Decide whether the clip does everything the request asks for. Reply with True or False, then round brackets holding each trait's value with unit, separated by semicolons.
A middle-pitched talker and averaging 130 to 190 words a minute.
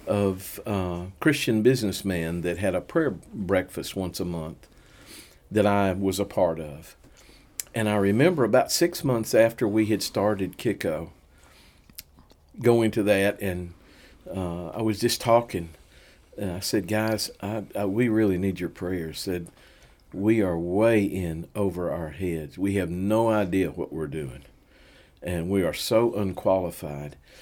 False (95 Hz; 155 wpm)